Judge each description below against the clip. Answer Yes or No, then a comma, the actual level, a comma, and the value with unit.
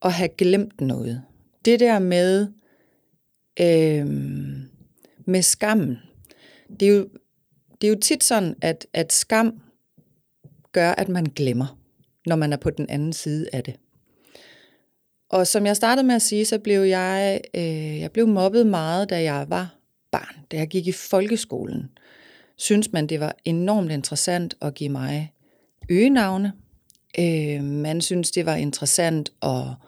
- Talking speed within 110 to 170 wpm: Yes, average, 150 wpm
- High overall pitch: No, medium, 170 Hz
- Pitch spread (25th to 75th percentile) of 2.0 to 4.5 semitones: No, wide, 5.5 semitones